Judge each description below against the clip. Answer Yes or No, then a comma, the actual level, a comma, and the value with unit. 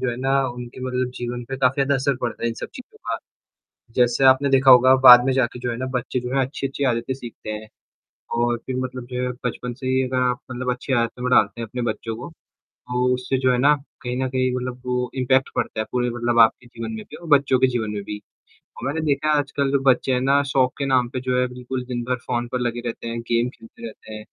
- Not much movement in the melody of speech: Yes, narrow, 1.6 semitones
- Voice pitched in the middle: No, low, 125 Hz